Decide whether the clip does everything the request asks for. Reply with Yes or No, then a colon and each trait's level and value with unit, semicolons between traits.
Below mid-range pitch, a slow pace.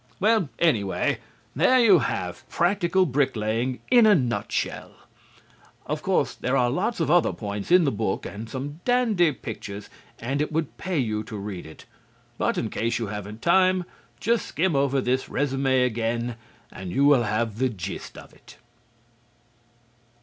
No: low, 130 Hz; average, 155 wpm